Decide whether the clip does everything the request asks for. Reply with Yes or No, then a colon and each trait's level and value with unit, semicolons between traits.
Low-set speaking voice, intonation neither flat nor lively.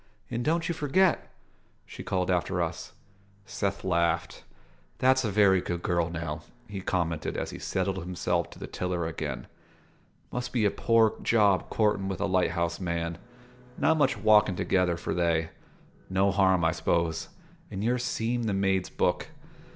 Yes: very low, 95 Hz; average, 4.0 semitones